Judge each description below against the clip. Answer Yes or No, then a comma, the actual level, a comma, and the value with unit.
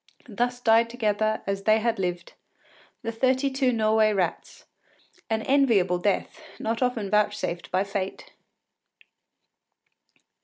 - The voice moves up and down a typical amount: Yes, average, 3.4 semitones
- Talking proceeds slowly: Yes, slow, 115 wpm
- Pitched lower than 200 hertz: No, high, 220 Hz